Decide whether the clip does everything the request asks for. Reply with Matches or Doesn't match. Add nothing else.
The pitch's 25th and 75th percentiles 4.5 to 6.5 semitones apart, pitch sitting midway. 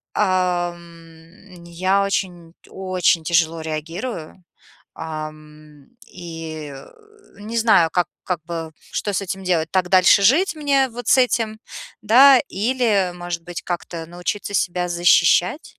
Doesn't match